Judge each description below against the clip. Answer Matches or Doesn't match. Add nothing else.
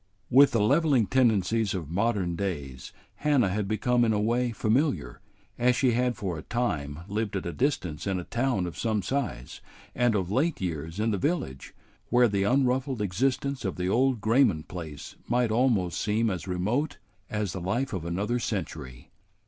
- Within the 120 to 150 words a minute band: Doesn't match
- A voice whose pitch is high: Doesn't match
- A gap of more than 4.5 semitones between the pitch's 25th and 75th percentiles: Matches